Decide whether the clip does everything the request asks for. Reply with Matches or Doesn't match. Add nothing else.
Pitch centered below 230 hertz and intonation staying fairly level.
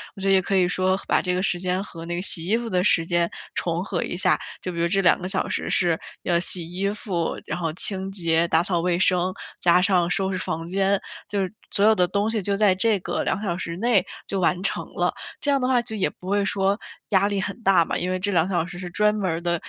Matches